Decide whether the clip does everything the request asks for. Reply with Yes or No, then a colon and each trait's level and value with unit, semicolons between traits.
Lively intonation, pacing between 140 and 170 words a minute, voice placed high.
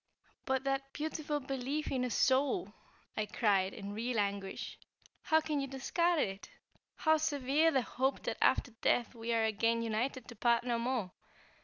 No: average, 3.8 semitones; average, 165 wpm; very high, 255 Hz